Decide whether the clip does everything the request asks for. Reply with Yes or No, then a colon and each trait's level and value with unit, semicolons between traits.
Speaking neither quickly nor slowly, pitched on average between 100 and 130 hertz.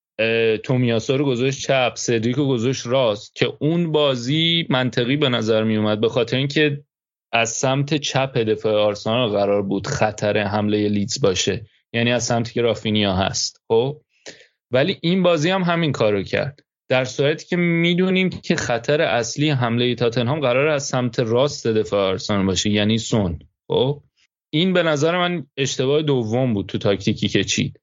No: fast, 165 wpm; low, 125 Hz